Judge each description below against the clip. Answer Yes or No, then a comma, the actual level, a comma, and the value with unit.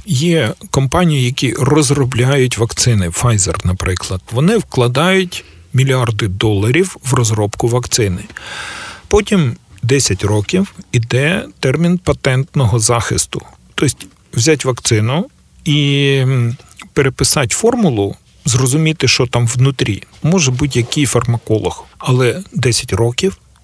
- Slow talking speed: Yes, slow, 95 wpm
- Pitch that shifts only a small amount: No, average, 4.3 semitones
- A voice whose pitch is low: Yes, low, 130 Hz